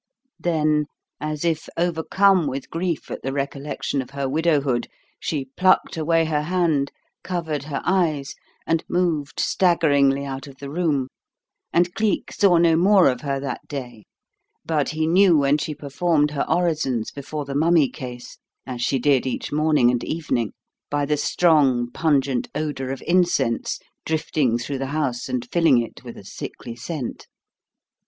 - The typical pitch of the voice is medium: Yes, medium, 150 Hz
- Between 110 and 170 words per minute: Yes, average, 155 wpm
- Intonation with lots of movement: No, average, 3.4 semitones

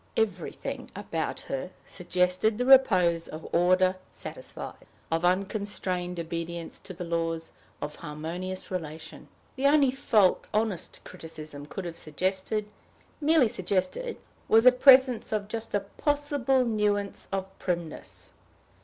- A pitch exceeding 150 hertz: Yes, medium, 185 Hz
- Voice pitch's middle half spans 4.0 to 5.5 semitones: Yes, average, 4.8 semitones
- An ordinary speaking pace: No, slow, 120 wpm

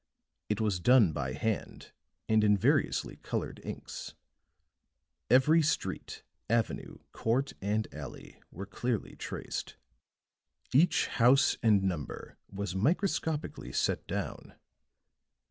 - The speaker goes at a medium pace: No, slow, 105 wpm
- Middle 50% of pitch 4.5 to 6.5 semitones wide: Yes, average, 5.0 semitones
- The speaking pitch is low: Yes, low, 110 Hz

